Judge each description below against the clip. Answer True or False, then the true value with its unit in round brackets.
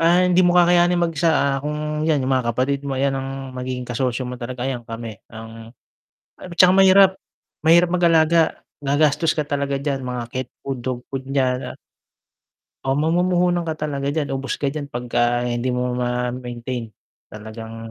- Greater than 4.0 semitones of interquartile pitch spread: True (4.5 semitones)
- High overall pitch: False (135 Hz)